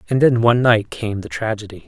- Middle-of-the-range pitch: No, low, 110 Hz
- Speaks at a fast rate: Yes, fast, 225 wpm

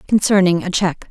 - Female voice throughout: Yes, female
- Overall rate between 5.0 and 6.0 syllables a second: No, 6.4 syllables/s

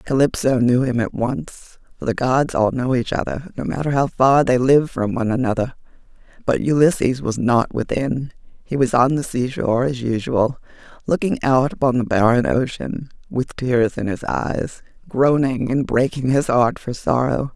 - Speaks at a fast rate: No, average, 170 wpm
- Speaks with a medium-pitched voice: No, low, 130 Hz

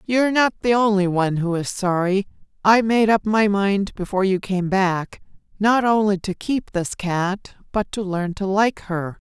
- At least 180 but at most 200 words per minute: Yes, average, 190 wpm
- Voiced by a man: No, female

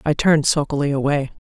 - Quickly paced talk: No, average, 165 wpm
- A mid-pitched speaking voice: Yes, medium, 145 Hz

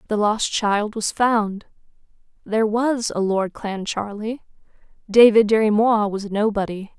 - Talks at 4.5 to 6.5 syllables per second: No, 4.1 syllables/s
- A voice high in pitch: Yes, high, 215 Hz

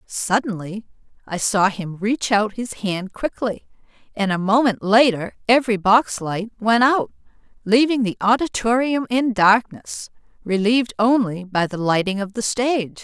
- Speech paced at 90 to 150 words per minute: Yes, average, 145 wpm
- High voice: Yes, high, 215 Hz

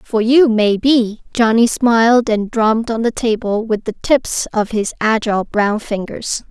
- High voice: Yes, high, 225 Hz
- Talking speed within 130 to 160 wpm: No, average, 175 wpm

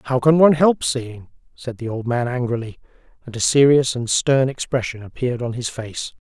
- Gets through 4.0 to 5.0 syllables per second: No, 5.3 syllables/s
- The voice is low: Yes, low, 125 Hz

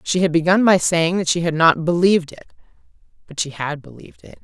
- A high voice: No, medium, 170 Hz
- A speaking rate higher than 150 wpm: Yes, fast, 205 wpm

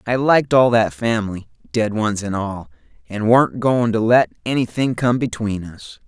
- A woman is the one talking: No, male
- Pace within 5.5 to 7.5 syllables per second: No, 4.7 syllables/s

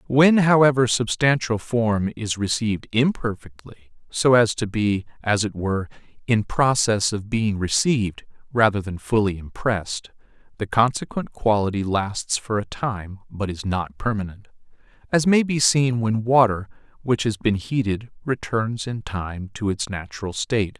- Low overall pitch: Yes, low, 110 Hz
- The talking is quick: No, average, 145 wpm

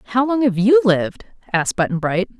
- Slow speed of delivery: No, average, 200 wpm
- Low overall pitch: No, high, 215 Hz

